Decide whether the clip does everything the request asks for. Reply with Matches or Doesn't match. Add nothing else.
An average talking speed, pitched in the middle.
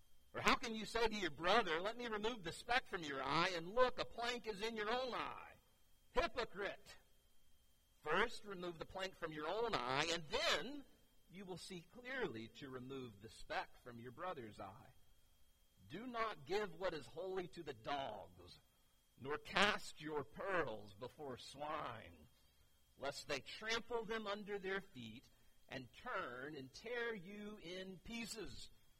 Matches